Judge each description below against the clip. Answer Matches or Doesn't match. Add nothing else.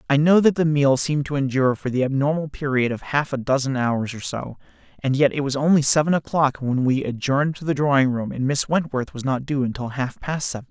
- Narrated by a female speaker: Doesn't match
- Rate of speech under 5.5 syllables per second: Doesn't match